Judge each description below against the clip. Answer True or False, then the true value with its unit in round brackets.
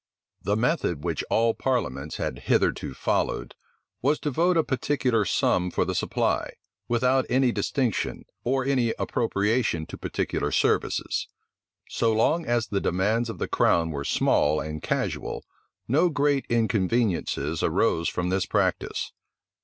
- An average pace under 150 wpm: True (140 wpm)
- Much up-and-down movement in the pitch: True (6.3 semitones)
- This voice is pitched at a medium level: False (115 Hz)